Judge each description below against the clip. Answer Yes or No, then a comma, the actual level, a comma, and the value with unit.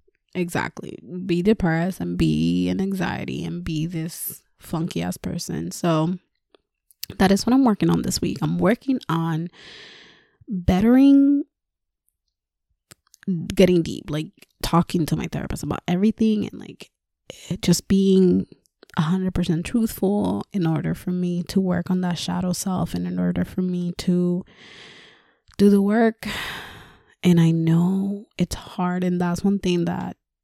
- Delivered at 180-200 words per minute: No, average, 145 wpm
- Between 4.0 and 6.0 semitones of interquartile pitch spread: No, average, 2.9 semitones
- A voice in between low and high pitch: Yes, medium, 180 Hz